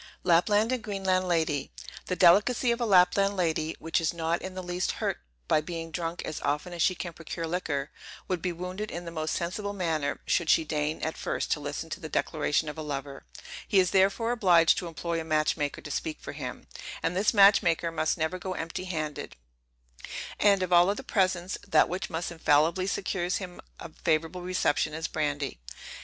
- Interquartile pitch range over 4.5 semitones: No, average, 2.8 semitones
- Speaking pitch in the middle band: Yes, medium, 170 Hz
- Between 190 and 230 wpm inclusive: Yes, average, 200 wpm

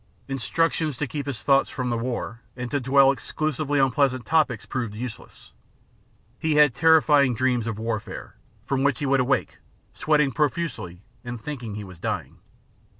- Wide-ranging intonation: No, average, 3.6 semitones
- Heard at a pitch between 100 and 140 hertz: Yes, low, 135 Hz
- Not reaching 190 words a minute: Yes, average, 160 wpm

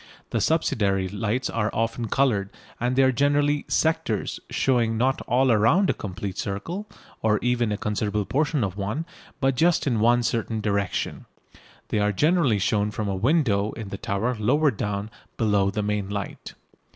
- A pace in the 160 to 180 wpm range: Yes, average, 165 wpm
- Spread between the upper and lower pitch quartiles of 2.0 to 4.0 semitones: No, average, 4.5 semitones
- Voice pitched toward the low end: Yes, low, 110 Hz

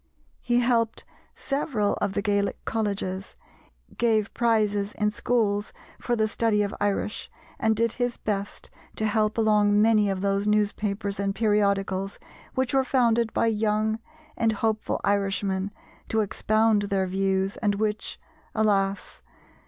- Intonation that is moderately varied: No, narrow, 1.8 semitones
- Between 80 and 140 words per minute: Yes, slow, 135 wpm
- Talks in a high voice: Yes, high, 210 Hz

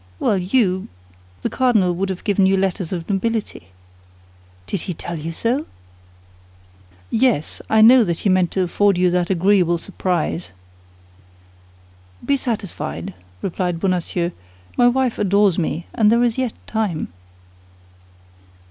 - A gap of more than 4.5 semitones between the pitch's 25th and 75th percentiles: No, average, 4.1 semitones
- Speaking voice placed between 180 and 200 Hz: Yes, high, 190 Hz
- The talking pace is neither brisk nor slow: No, slow, 130 wpm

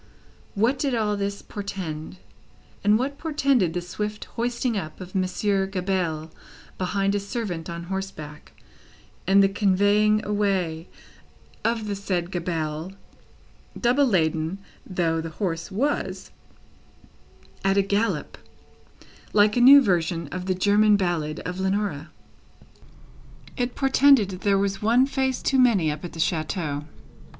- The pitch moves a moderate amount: Yes, average, 3.6 semitones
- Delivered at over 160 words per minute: No, slow, 135 wpm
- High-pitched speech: Yes, high, 195 Hz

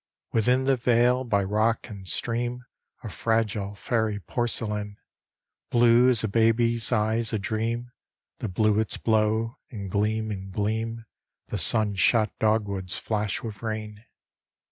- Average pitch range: No, narrow, 1.9 semitones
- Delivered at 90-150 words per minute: Yes, slow, 135 wpm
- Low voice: Yes, low, 110 Hz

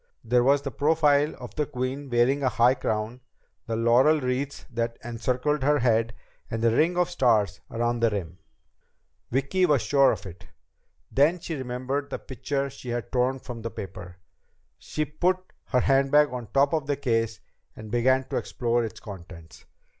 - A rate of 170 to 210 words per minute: Yes, average, 175 wpm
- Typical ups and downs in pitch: Yes, average, 3.6 semitones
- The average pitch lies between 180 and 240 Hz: No, low, 125 Hz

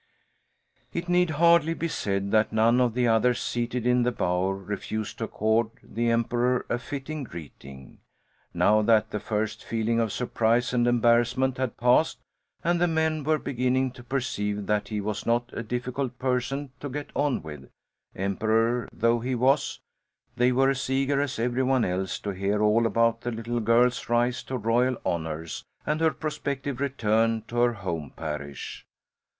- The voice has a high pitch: No, low, 120 Hz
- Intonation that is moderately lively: Yes, average, 3.3 semitones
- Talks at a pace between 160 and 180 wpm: Yes, average, 170 wpm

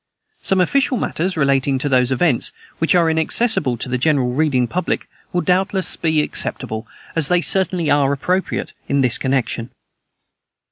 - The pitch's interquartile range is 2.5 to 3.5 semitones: No, wide, 5.4 semitones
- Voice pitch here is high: No, medium, 150 Hz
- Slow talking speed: No, average, 150 wpm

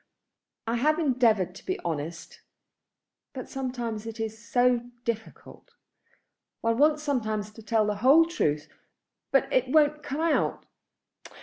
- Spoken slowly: Yes, slow, 130 wpm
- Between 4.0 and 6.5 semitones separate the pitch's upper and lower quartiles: Yes, average, 4.5 semitones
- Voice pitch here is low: No, high, 235 Hz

